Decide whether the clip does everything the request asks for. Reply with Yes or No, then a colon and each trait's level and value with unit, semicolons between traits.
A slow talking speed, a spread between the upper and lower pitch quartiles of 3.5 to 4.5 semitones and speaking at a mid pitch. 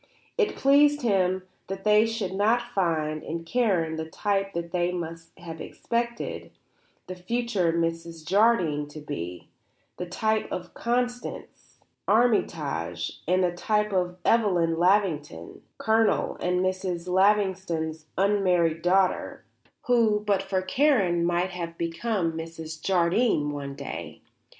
Yes: slow, 125 wpm; average, 4.1 semitones; medium, 180 Hz